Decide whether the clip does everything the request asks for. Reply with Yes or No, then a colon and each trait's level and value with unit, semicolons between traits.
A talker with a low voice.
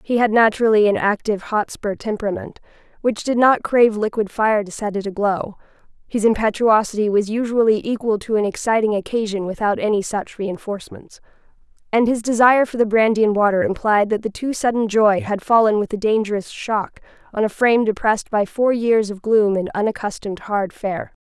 No: high, 215 Hz